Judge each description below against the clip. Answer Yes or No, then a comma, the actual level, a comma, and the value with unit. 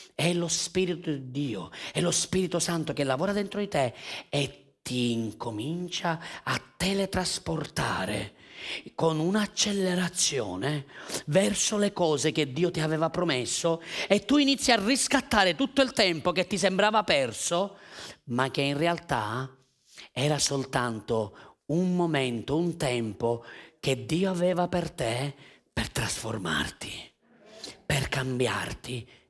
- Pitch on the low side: No, medium, 165 Hz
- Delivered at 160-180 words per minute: No, average, 125 wpm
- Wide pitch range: Yes, wide, 5.9 semitones